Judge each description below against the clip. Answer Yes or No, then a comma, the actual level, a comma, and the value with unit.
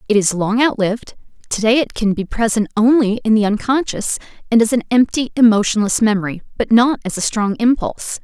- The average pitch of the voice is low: No, high, 220 Hz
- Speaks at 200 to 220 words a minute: No, average, 190 wpm